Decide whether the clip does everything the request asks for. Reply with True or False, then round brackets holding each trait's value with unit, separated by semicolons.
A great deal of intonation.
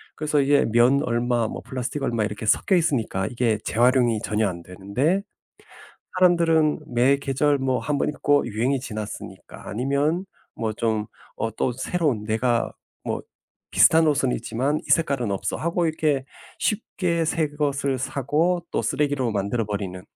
False (4.9 semitones)